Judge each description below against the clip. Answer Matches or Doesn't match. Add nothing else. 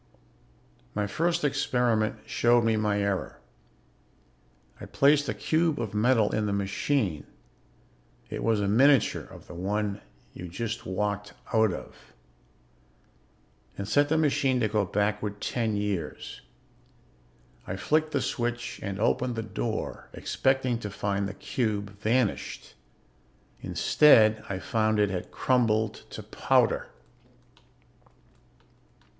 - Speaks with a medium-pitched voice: Doesn't match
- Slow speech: Matches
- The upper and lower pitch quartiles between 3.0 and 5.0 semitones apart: Matches